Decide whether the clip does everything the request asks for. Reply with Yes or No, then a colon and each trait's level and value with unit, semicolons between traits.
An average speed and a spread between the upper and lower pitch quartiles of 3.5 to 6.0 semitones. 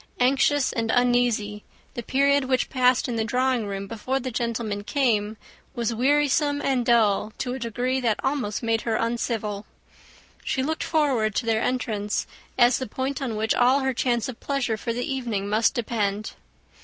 No: average, 170 wpm; average, 3.1 semitones